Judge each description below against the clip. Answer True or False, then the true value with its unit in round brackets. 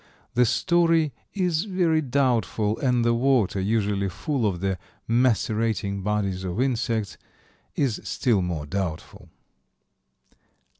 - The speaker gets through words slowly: True (110 wpm)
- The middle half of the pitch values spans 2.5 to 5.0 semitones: False (5.5 semitones)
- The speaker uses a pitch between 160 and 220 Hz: False (115 Hz)